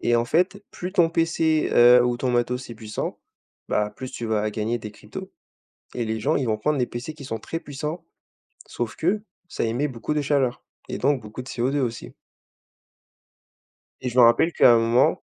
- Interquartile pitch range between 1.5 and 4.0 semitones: No, average, 4.4 semitones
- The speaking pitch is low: Yes, low, 125 Hz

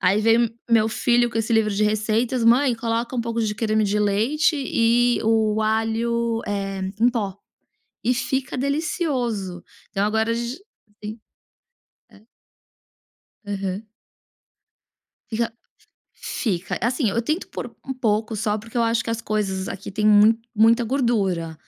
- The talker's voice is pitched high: Yes, high, 225 Hz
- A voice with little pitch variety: Yes, narrow, 2.1 semitones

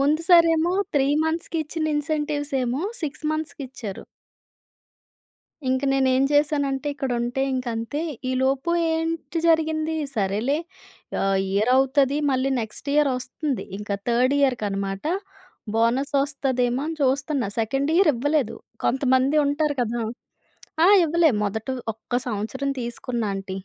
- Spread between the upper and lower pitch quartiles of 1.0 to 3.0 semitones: No, average, 3.8 semitones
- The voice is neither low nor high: No, very high, 270 Hz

